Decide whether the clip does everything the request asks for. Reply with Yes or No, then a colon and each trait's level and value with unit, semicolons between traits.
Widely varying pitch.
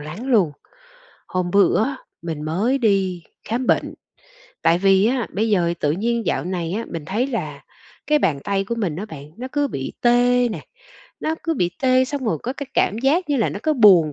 Yes: wide, 6.3 semitones